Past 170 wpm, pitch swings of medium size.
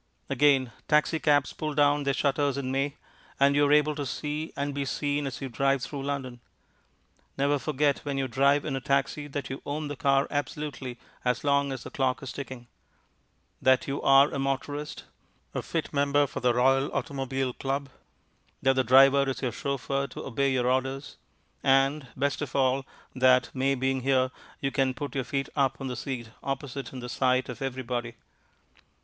No: average, 180 wpm; narrow, 1.4 semitones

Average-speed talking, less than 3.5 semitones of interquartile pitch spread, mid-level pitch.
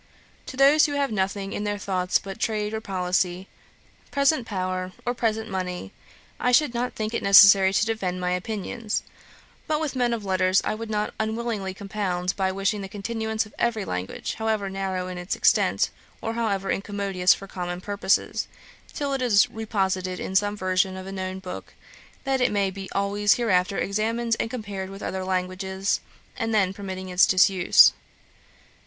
No: average, 175 wpm; average, 2.9 semitones; high, 200 Hz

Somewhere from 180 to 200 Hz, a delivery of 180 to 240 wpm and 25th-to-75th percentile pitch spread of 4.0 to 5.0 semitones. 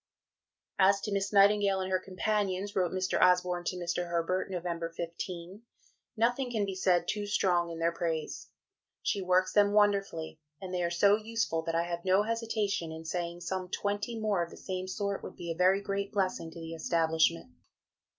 No: medium, 185 Hz; average, 185 wpm; average, 2.8 semitones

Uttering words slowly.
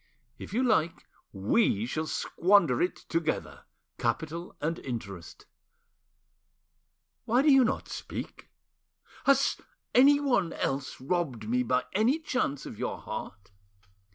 Yes: slow, 115 wpm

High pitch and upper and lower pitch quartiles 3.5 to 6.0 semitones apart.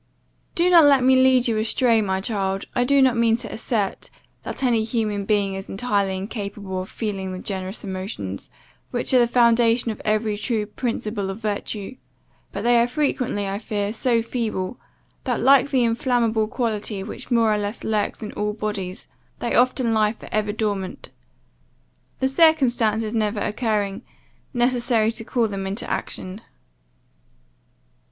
No: high, 220 Hz; average, 3.0 semitones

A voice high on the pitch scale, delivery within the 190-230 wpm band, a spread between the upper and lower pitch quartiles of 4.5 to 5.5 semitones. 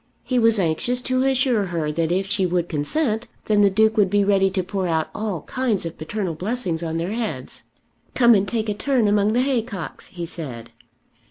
Yes: high, 200 Hz; average, 200 wpm; average, 4.8 semitones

